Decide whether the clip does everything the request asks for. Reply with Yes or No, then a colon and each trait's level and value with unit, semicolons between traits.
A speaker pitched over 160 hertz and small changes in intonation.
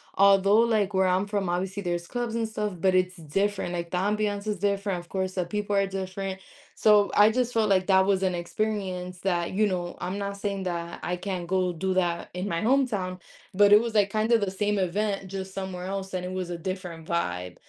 Yes: high, 190 Hz; narrow, 2.2 semitones